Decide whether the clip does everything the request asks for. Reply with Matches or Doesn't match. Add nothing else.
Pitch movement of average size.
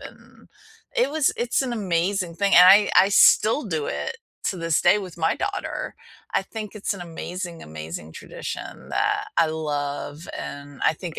Matches